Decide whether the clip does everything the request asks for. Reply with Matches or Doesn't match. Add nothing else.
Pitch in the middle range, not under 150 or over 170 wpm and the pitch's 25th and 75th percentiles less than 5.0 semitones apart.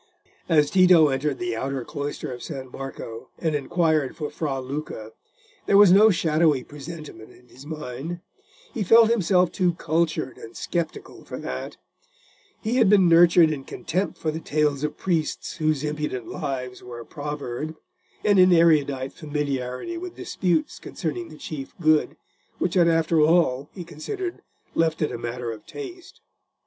Matches